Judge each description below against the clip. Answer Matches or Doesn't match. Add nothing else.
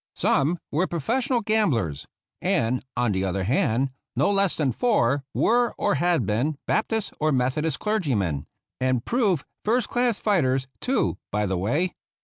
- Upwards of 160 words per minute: Doesn't match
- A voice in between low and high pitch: Matches